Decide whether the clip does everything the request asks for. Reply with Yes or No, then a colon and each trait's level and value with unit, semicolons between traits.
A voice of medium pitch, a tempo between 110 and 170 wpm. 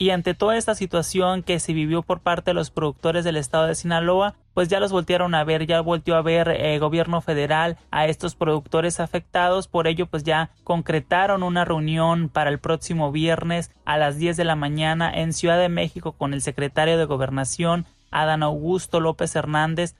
No: medium, 165 Hz; fast, 190 wpm